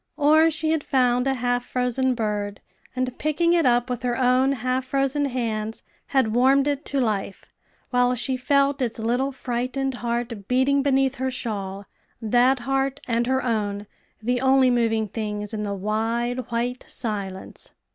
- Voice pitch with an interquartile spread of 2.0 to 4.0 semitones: Yes, average, 3.0 semitones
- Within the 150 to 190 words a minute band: Yes, average, 160 wpm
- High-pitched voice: Yes, very high, 250 Hz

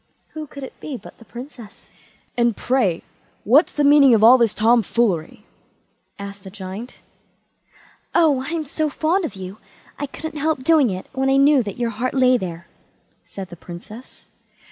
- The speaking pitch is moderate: No, high, 245 Hz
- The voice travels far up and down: Yes, wide, 5.8 semitones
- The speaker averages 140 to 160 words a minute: No, average, 170 wpm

